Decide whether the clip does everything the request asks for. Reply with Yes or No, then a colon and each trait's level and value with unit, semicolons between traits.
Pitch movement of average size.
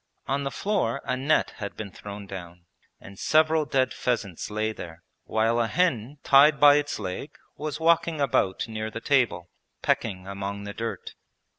No: wide, 6.3 semitones